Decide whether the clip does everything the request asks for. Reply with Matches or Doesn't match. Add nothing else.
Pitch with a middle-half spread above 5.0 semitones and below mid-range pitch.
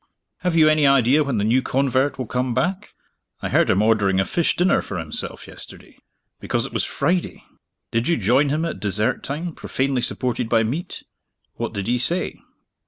Matches